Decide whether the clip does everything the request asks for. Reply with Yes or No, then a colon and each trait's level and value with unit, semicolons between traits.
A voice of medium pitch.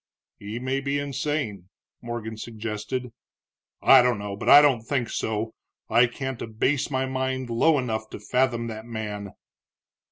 No: low, 120 Hz